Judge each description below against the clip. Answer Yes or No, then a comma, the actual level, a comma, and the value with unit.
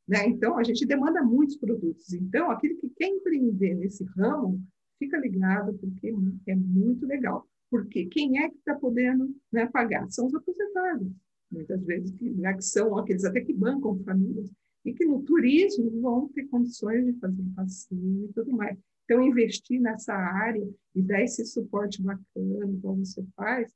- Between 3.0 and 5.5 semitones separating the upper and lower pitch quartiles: Yes, average, 4.7 semitones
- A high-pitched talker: Yes, high, 225 Hz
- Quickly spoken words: No, average, 170 wpm